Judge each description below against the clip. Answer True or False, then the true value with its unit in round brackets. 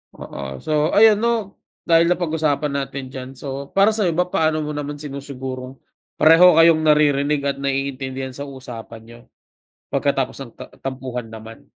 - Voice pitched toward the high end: False (140 Hz)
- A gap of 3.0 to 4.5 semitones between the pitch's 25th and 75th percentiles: True (3.6 semitones)